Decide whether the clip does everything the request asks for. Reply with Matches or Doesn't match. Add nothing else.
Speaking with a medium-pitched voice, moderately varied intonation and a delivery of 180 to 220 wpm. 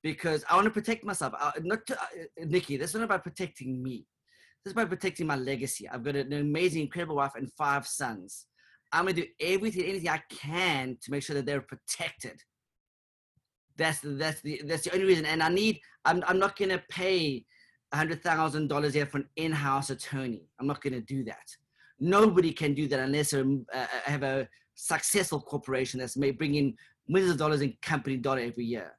Matches